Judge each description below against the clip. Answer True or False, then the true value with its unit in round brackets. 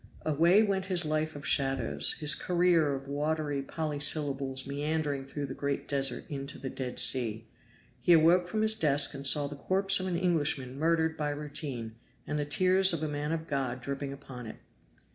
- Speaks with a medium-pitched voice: True (145 Hz)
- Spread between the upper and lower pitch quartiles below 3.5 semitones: True (2.9 semitones)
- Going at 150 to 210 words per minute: True (180 wpm)